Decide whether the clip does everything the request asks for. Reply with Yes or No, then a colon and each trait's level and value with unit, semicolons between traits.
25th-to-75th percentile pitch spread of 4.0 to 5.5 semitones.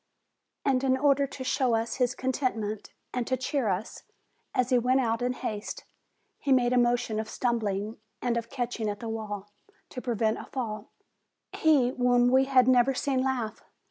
No: narrow, 2.5 semitones